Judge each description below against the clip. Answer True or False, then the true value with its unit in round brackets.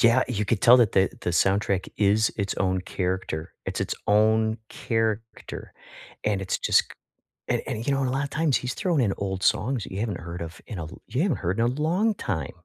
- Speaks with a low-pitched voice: True (110 Hz)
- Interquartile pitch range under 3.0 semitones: False (4.6 semitones)